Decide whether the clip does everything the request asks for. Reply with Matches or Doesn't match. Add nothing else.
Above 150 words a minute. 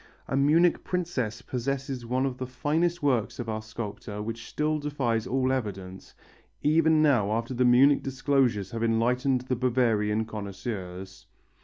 Doesn't match